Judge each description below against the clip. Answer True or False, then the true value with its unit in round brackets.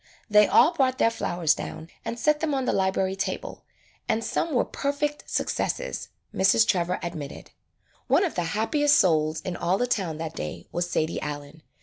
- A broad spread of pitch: True (8.2 semitones)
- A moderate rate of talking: True (185 wpm)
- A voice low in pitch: False (190 Hz)